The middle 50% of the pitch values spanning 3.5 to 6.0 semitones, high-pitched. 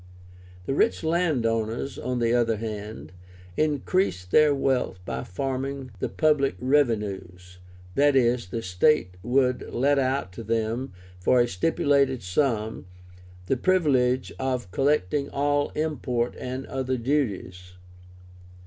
No: average, 4.1 semitones; low, 130 Hz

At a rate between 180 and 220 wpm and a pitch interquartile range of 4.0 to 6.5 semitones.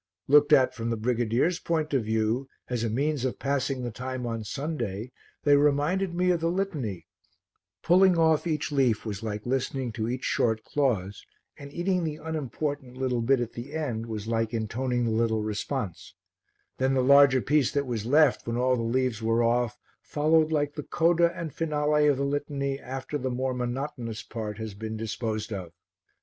Yes: average, 185 wpm; average, 4.5 semitones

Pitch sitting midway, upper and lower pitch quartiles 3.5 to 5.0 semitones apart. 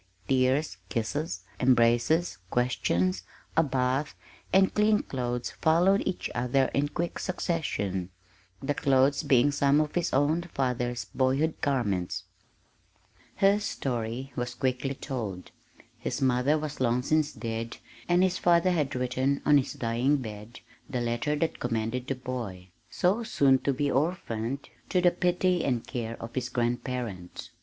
No: low, 130 Hz; average, 4.2 semitones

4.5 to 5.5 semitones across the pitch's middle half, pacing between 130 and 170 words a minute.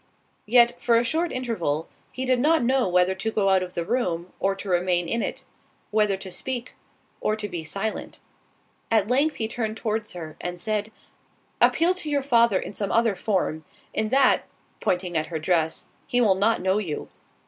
No: average, 4.8 semitones; average, 185 wpm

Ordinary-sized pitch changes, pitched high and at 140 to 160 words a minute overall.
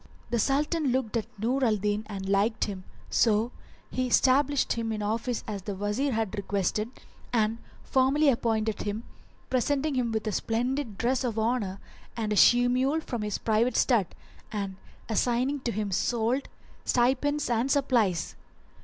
Yes: average, 3.5 semitones; high, 230 Hz; average, 155 wpm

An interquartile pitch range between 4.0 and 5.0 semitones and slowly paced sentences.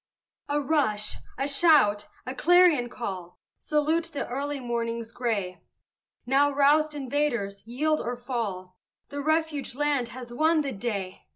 Yes: average, 4.3 semitones; slow, 130 wpm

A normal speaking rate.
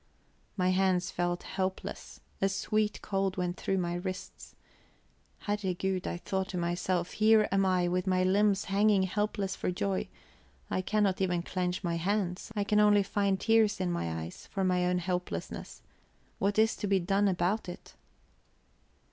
Yes: average, 160 wpm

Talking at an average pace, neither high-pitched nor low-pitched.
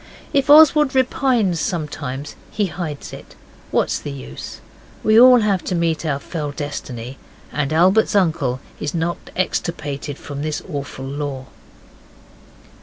No: slow, 130 wpm; medium, 155 Hz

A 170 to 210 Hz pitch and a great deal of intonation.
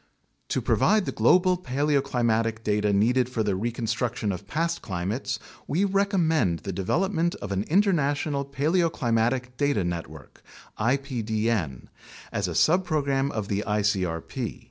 No: low, 125 Hz; wide, 6.5 semitones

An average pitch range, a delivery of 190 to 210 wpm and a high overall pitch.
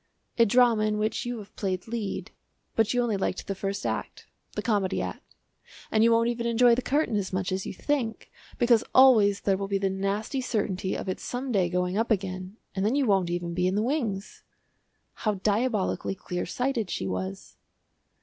Yes: average, 3.6 semitones; average, 200 wpm; high, 210 Hz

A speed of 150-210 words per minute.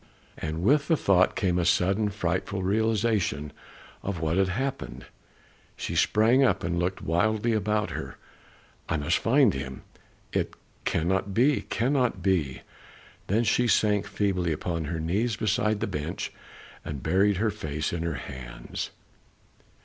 No: average, 140 wpm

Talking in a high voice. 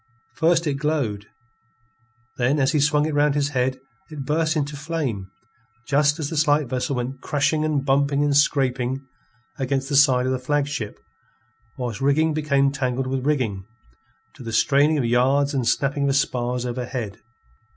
No: medium, 140 Hz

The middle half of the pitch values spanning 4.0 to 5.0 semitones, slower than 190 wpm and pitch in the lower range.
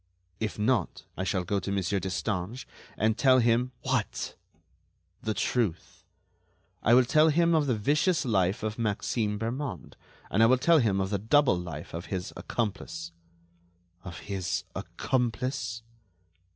Yes: average, 4.7 semitones; average, 145 wpm; low, 110 Hz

